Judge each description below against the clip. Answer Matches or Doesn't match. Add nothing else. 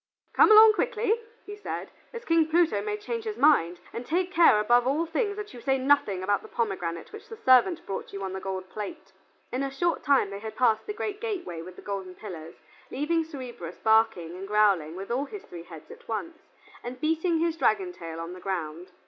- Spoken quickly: Matches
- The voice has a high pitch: Matches